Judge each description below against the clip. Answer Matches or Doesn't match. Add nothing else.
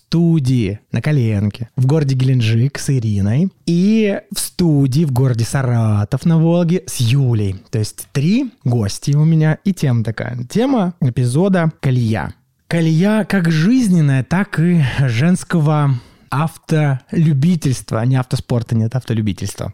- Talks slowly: Doesn't match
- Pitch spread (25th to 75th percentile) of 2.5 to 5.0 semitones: Doesn't match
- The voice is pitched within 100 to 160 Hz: Matches